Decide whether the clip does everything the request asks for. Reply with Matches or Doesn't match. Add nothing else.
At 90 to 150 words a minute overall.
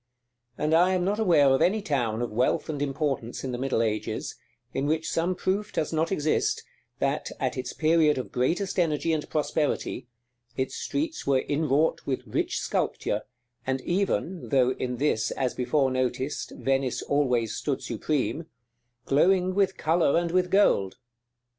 Doesn't match